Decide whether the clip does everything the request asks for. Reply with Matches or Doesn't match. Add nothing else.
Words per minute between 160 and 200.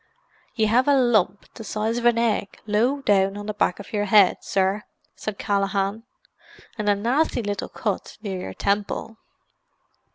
Matches